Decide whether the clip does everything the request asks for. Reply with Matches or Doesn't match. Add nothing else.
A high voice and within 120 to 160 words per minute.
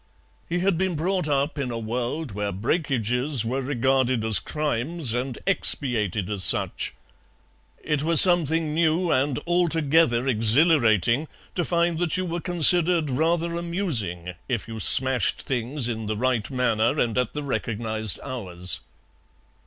Doesn't match